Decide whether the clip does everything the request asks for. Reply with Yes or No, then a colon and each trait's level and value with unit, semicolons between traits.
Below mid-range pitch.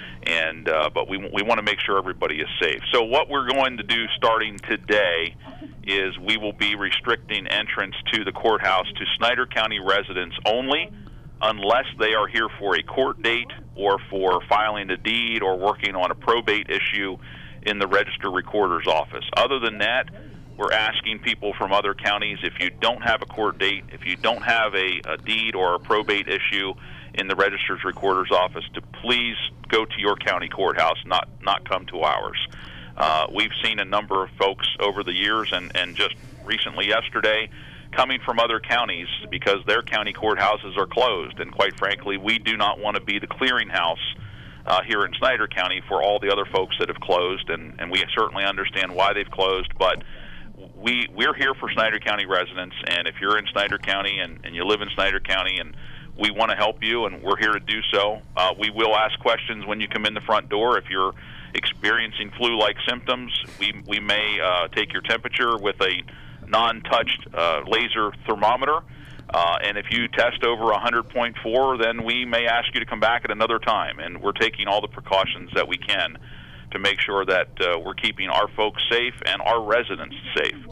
Yes: low, 105 Hz